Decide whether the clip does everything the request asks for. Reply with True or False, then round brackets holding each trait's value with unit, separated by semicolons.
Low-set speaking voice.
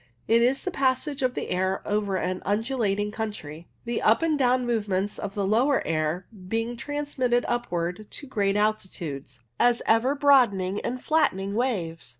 False (220 Hz)